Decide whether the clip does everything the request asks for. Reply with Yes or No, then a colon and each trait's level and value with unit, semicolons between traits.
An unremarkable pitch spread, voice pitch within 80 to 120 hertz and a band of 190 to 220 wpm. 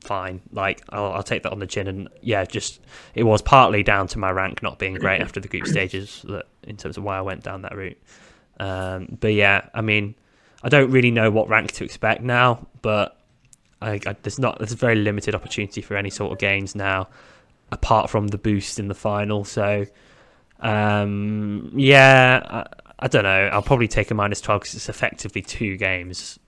No: narrow, 2.0 semitones; low, 105 Hz; fast, 205 wpm